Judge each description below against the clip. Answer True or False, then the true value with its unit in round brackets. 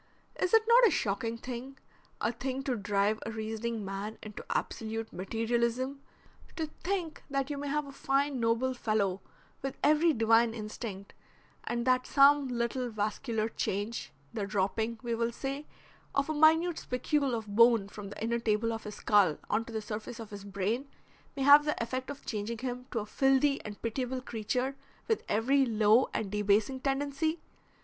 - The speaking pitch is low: False (235 Hz)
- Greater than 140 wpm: True (170 wpm)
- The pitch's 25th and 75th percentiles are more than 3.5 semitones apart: True (4.1 semitones)